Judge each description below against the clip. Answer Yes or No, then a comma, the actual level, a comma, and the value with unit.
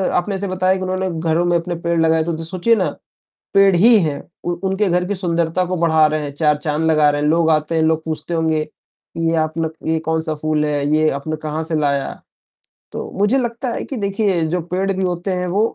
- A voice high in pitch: No, medium, 165 Hz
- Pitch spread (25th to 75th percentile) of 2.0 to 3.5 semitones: Yes, average, 2.9 semitones